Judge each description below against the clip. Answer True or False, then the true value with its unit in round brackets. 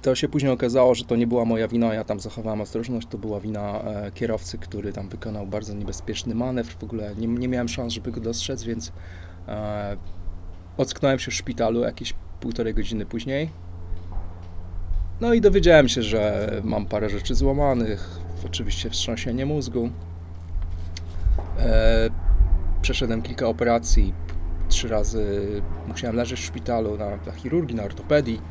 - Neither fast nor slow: True (150 wpm)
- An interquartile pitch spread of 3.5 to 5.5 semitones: True (5.1 semitones)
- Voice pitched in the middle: False (105 Hz)